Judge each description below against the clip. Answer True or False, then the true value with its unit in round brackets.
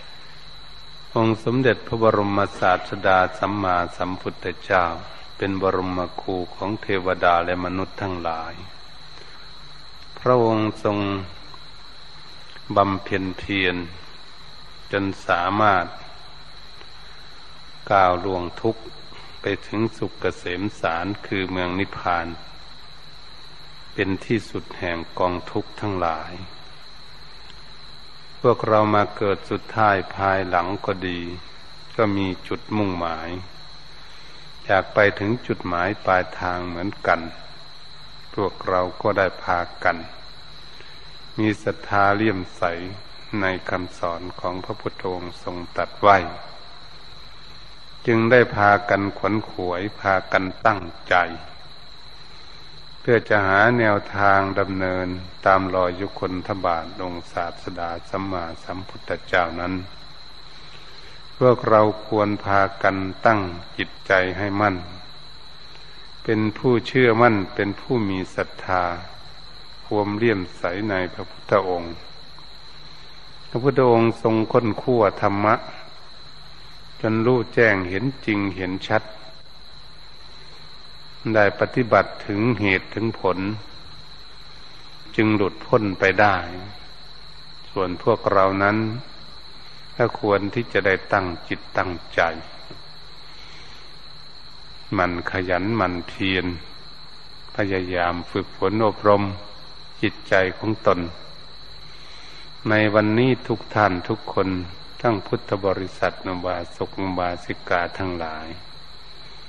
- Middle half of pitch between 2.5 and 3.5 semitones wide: True (3.1 semitones)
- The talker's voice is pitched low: True (95 Hz)